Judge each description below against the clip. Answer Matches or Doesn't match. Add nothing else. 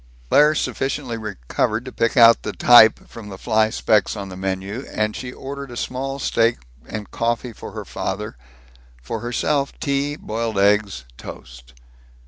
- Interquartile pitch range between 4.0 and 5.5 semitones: Doesn't match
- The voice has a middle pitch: Doesn't match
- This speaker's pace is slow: Doesn't match